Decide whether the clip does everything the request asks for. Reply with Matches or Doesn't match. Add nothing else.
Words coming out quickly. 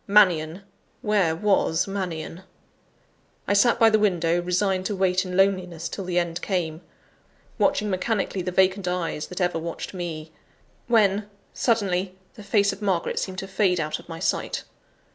Doesn't match